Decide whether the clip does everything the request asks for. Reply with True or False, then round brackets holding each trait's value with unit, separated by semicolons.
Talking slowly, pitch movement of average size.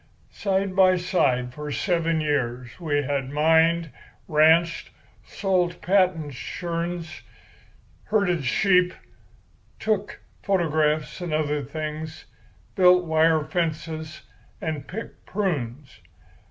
True (95 wpm; 3.2 semitones)